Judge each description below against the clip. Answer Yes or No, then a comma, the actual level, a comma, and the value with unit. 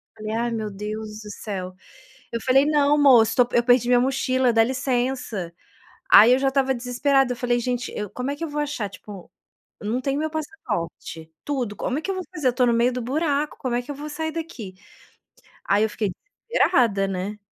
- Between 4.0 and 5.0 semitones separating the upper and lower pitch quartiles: Yes, average, 4.4 semitones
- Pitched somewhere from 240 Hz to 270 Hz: Yes, high, 245 Hz